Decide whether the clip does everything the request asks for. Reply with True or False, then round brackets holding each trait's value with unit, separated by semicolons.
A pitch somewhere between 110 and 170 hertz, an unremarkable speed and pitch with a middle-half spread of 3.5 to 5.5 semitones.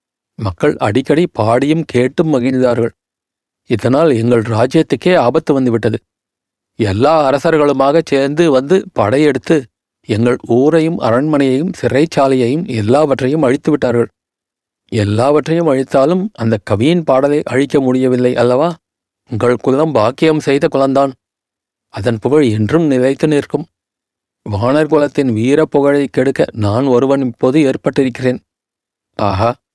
True (135 Hz; 100 wpm; 4.1 semitones)